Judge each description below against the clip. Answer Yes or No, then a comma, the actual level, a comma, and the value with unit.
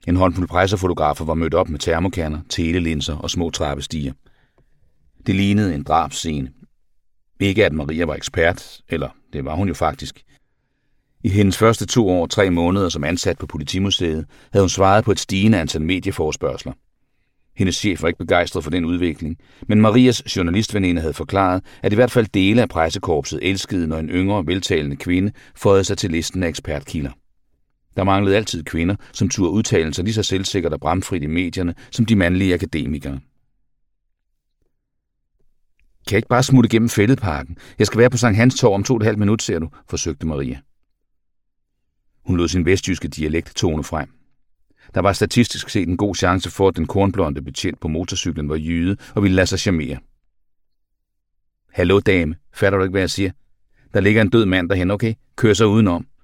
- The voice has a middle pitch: No, very low, 95 Hz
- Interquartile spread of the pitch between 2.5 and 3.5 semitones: No, average, 3.9 semitones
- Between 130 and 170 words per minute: No, average, 180 wpm